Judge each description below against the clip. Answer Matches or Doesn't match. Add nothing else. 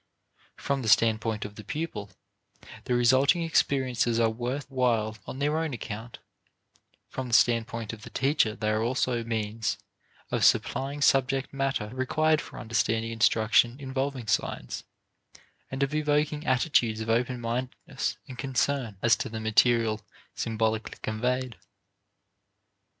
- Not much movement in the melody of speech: Doesn't match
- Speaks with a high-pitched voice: Doesn't match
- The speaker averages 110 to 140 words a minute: Matches